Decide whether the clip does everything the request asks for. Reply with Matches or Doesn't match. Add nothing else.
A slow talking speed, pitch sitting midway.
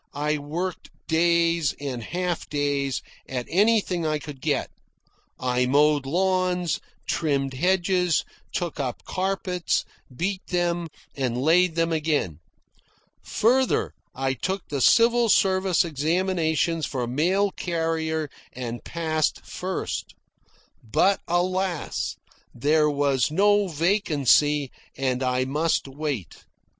Matches